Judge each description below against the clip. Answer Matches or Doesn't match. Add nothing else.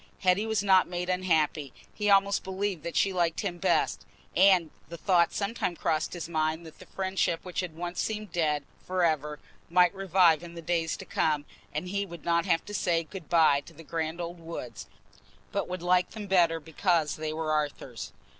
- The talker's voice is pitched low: Doesn't match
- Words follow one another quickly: Doesn't match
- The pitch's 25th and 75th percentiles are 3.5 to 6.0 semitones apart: Doesn't match